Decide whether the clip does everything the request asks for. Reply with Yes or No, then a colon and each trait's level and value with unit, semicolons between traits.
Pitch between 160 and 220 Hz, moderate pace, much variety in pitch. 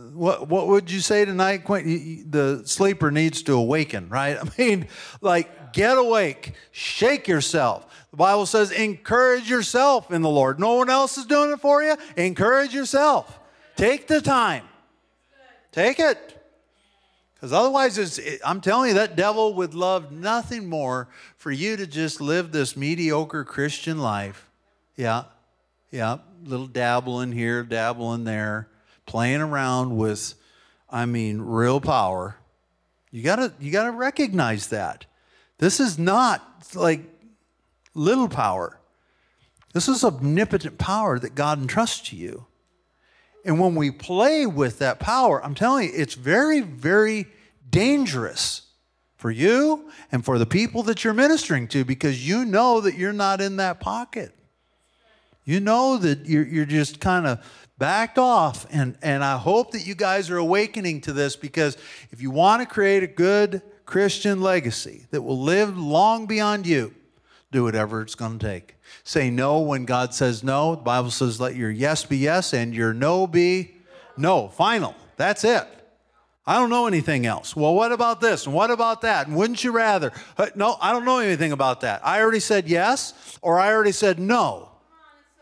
Yes: medium, 170 Hz; average, 160 wpm; wide, 8.1 semitones